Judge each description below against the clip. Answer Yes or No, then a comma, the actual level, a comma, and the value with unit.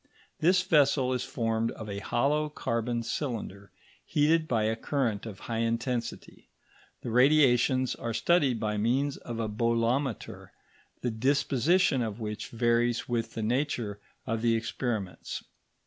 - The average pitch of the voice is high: No, low, 120 Hz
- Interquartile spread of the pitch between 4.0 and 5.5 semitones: No, average, 3.3 semitones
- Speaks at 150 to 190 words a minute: No, slow, 135 wpm